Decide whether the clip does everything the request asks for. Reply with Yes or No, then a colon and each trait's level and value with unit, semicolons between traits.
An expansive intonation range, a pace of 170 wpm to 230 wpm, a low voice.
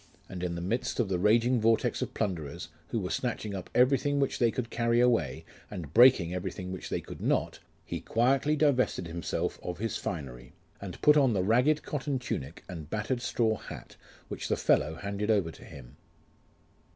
Yes: wide, 5.8 semitones; average, 185 wpm; low, 110 Hz